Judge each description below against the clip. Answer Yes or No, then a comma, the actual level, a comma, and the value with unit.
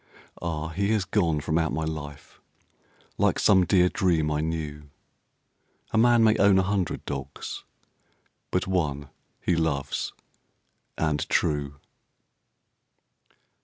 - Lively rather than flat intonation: No, average, 4.0 semitones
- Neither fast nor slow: No, slow, 120 wpm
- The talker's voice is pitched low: Yes, very low, 80 Hz